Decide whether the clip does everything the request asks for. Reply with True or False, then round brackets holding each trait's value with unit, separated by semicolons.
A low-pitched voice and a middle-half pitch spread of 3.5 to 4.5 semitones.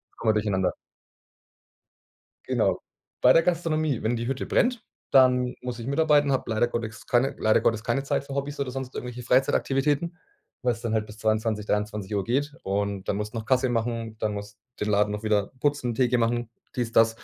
True (120 Hz; 3.9 semitones)